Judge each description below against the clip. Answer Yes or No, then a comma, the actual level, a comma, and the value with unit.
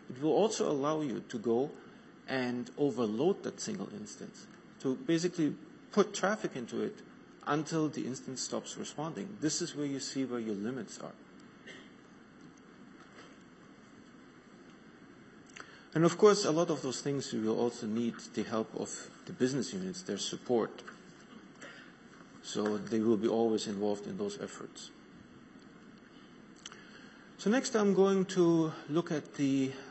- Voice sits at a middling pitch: Yes, medium, 145 Hz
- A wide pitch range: Yes, wide, 7.3 semitones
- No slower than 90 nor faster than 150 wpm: Yes, average, 140 wpm